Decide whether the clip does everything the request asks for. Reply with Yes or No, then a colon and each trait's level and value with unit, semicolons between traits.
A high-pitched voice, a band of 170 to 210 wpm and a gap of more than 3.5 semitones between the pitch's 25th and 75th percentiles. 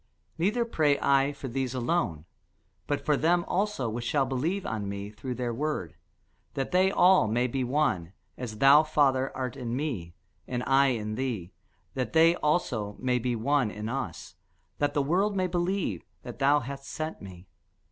No: low, 135 Hz; average, 175 wpm; average, 4.7 semitones